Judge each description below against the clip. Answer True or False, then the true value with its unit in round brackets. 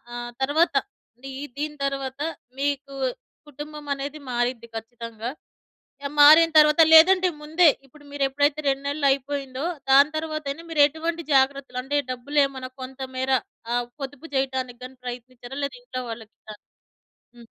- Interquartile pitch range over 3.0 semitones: False (2.7 semitones)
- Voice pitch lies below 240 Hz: False (275 Hz)